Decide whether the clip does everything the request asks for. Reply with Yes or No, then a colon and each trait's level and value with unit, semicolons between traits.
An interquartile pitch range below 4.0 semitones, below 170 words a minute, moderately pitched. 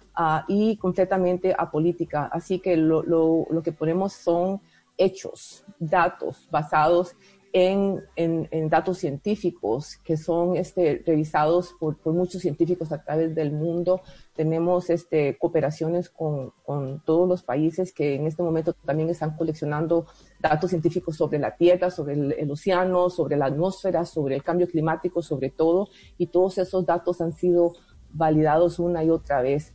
Yes: narrow, 2.4 semitones; average, 155 wpm; medium, 170 Hz